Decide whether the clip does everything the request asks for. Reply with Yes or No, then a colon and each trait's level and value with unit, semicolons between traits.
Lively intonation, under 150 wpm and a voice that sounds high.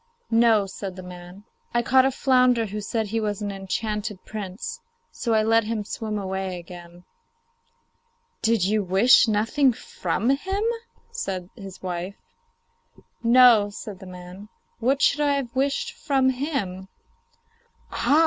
No: average, 4.8 semitones; average, 140 wpm; high, 215 Hz